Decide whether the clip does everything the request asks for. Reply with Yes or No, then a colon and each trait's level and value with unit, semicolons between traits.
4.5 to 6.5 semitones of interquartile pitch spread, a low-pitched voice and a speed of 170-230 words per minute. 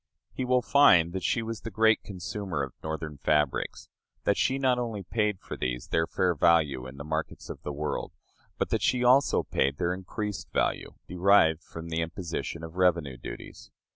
Yes: average, 5.2 semitones; very low, 85 Hz; average, 185 wpm